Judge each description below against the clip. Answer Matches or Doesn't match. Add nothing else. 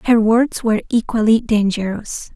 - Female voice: Matches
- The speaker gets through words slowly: Matches